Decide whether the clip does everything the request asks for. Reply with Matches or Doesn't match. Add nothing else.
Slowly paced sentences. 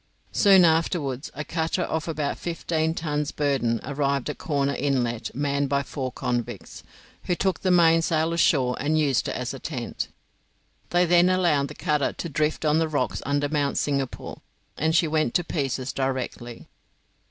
Doesn't match